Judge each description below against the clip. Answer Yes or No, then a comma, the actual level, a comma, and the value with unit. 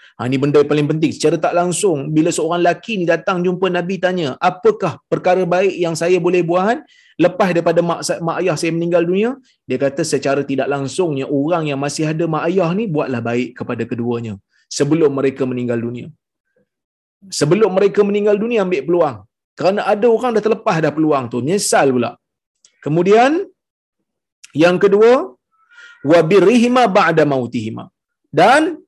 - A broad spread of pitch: Yes, wide, 6.0 semitones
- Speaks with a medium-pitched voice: Yes, medium, 170 Hz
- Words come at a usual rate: No, fast, 155 wpm